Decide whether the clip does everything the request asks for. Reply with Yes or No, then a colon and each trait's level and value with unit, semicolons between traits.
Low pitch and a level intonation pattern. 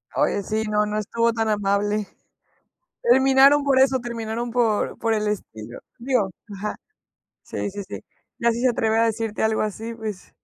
No: high, 220 Hz; narrow, 2.0 semitones